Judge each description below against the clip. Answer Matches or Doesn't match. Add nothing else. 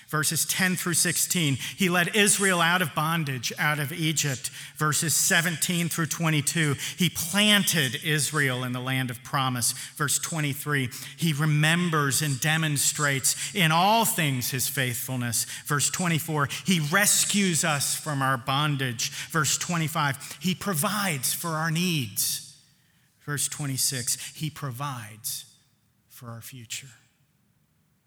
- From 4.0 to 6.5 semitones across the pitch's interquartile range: Doesn't match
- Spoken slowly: Matches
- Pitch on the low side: Doesn't match